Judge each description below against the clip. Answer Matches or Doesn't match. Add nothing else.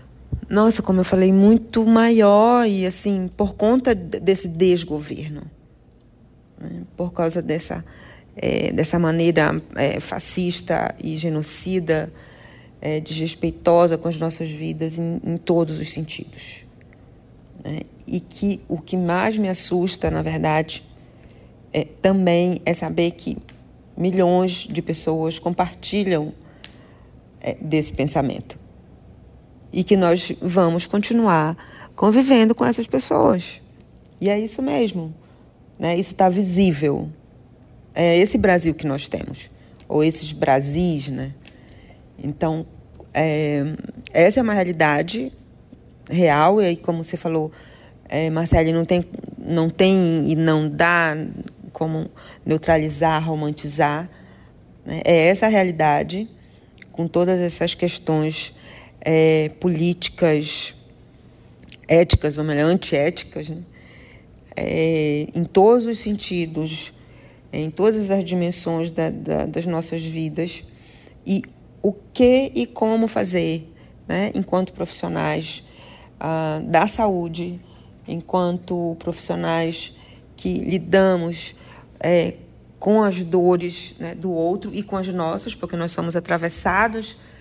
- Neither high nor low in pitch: Matches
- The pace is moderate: Doesn't match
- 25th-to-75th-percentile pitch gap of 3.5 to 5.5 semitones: Doesn't match